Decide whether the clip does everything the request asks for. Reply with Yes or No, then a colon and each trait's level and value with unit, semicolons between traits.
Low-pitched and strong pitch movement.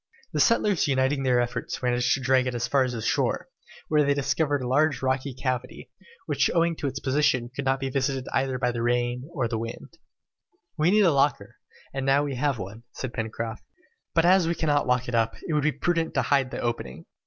No: low, 130 Hz; average, 2.9 semitones